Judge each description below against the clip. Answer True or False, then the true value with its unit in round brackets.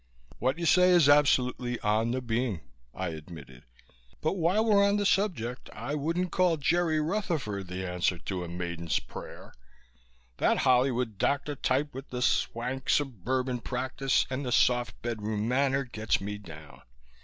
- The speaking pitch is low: True (125 Hz)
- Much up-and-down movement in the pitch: True (6.0 semitones)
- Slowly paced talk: False (155 wpm)